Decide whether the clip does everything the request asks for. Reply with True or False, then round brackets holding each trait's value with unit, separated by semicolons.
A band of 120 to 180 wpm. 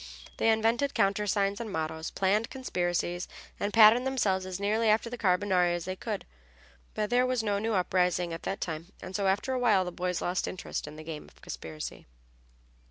False (190 wpm)